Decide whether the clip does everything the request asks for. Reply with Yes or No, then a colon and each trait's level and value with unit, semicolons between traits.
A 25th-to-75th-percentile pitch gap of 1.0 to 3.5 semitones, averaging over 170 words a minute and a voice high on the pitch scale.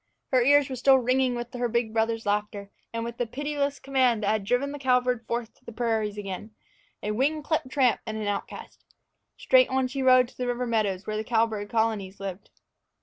Yes: average, 3.2 semitones; fast, 205 wpm; high, 235 Hz